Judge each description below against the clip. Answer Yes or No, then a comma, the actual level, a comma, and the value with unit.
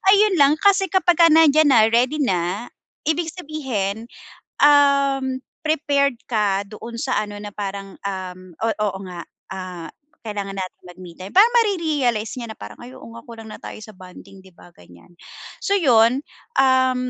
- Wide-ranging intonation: Yes, wide, 6.6 semitones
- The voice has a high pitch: Yes, high, 235 Hz